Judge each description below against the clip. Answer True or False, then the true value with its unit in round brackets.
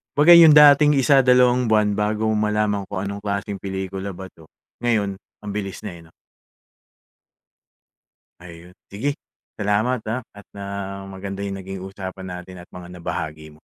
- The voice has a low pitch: True (100 Hz)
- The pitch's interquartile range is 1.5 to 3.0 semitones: True (2.6 semitones)